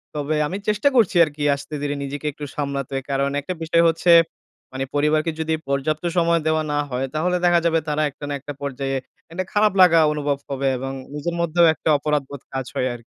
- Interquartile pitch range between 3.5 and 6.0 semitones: No, average, 3.1 semitones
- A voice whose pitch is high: No, medium, 150 Hz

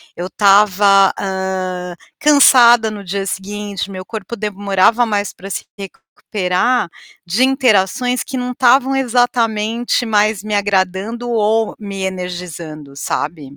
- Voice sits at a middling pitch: No, high, 205 Hz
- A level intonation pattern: No, average, 3.8 semitones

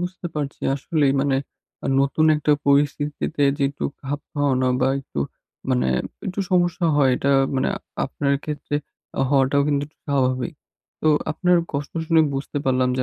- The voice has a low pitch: No, medium, 145 Hz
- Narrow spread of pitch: Yes, narrow, 2.1 semitones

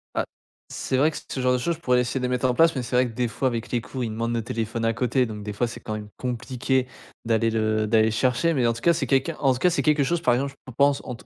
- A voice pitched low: Yes, low, 125 Hz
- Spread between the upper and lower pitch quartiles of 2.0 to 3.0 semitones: Yes, average, 2.7 semitones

